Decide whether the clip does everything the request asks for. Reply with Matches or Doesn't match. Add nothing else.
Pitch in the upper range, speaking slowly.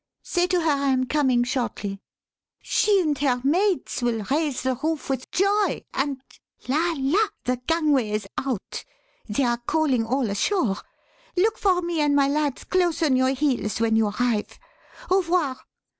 Doesn't match